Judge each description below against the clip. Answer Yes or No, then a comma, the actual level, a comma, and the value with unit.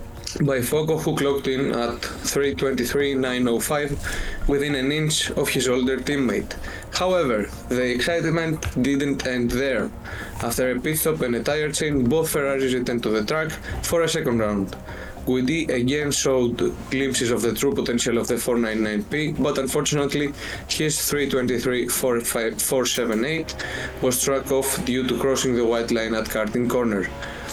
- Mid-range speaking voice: No, low, 130 Hz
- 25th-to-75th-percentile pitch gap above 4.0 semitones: No, average, 3.2 semitones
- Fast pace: No, average, 140 wpm